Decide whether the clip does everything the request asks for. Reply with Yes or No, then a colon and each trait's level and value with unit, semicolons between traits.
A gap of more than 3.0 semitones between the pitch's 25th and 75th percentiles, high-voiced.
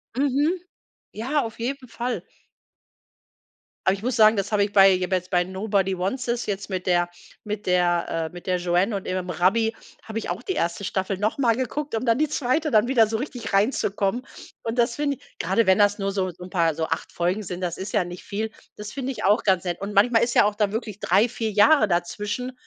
Yes: average, 4.1 semitones; high, 210 Hz